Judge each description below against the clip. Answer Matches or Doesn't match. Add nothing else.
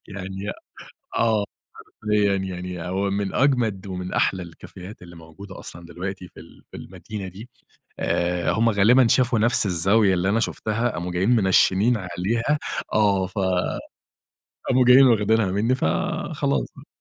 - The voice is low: Matches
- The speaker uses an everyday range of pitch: Matches